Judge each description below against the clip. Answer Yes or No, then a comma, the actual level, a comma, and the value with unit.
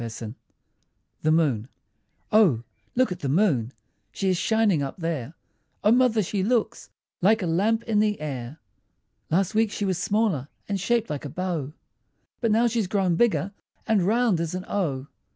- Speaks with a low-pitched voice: No, medium, 185 Hz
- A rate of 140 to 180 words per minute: Yes, average, 170 wpm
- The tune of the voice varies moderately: No, wide, 6.1 semitones